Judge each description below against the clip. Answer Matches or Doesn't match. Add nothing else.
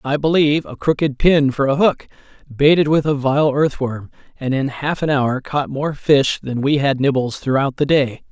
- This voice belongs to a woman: Doesn't match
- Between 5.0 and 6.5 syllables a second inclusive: Doesn't match